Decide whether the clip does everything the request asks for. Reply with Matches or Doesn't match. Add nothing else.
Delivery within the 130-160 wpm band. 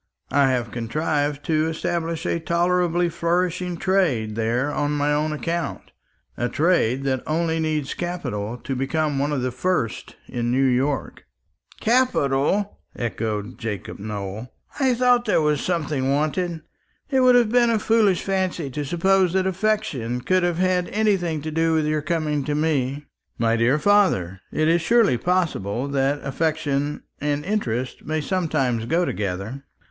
Matches